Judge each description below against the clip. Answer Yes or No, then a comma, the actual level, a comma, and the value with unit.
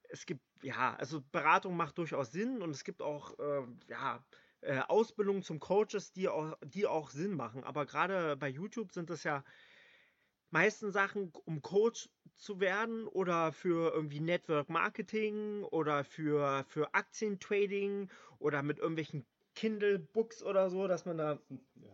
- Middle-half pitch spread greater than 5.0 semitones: Yes, wide, 5.4 semitones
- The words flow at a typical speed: Yes, average, 150 wpm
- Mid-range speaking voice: Yes, medium, 175 Hz